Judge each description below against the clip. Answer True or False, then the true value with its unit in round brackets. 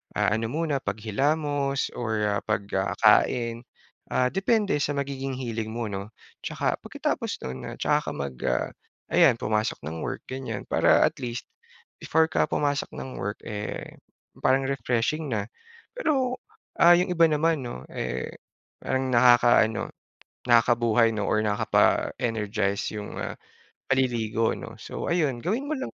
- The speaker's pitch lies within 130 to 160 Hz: False (120 Hz)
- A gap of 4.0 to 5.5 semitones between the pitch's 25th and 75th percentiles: True (5.0 semitones)